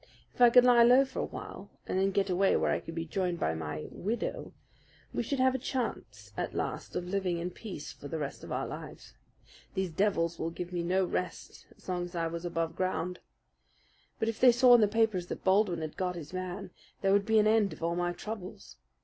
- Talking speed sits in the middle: No, fast, 230 wpm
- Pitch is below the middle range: No, medium, 185 Hz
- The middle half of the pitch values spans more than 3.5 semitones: Yes, average, 4.1 semitones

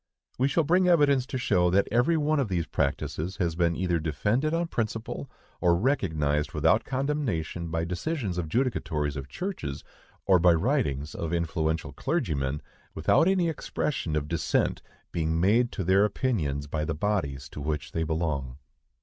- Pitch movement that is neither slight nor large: No, wide, 8.6 semitones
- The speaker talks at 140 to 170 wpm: Yes, average, 160 wpm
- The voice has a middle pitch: No, very low, 90 Hz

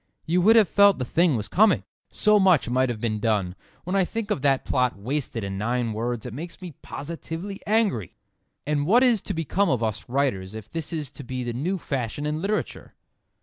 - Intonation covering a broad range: Yes, wide, 7.6 semitones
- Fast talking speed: Yes, fast, 210 wpm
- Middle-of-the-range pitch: Yes, medium, 145 Hz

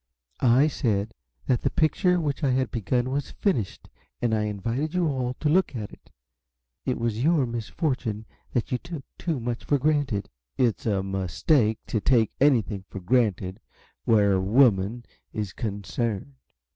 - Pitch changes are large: No, average, 4.8 semitones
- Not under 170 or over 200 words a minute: No, average, 160 wpm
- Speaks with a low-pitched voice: Yes, low, 120 Hz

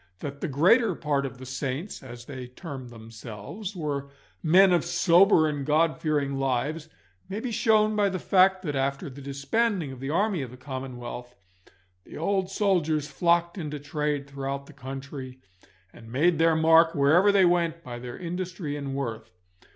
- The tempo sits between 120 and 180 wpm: Yes, average, 170 wpm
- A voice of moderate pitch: Yes, medium, 150 Hz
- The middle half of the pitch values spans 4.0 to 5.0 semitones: Yes, average, 4.5 semitones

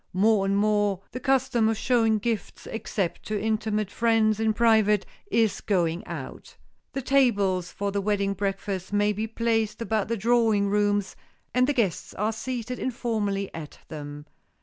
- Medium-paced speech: Yes, average, 155 wpm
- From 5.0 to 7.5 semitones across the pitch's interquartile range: No, narrow, 2.4 semitones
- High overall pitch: Yes, high, 215 Hz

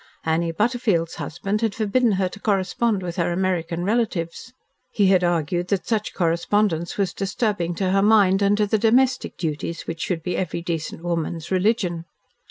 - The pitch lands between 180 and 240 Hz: Yes, medium, 185 Hz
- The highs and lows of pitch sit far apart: No, average, 3.6 semitones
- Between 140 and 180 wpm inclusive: Yes, average, 170 wpm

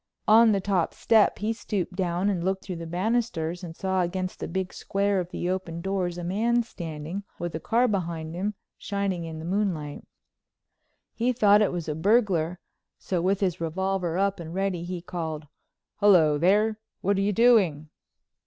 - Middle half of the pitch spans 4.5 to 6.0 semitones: No, average, 3.2 semitones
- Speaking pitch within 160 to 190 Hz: Yes, medium, 185 Hz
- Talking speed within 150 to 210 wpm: Yes, average, 180 wpm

